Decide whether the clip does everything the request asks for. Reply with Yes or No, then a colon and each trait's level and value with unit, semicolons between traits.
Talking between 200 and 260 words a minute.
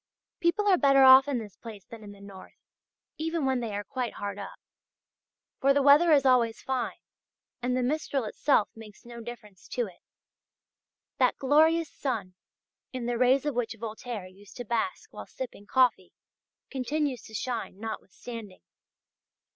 No: average, 160 wpm